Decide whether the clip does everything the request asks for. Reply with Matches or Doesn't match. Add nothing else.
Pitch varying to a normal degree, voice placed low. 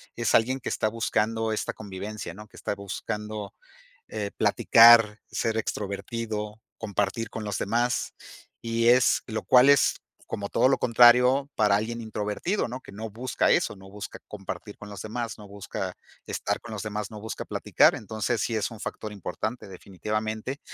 Doesn't match